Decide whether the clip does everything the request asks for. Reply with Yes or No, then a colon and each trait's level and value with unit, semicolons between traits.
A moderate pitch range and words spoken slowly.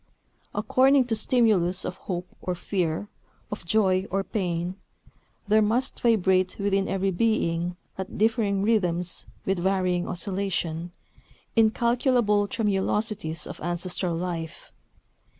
Yes: average, 3.5 semitones; slow, 110 wpm